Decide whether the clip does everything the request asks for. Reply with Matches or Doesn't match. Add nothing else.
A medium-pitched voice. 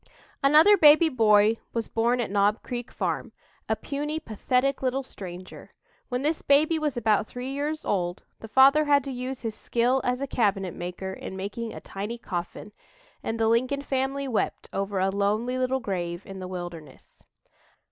Doesn't match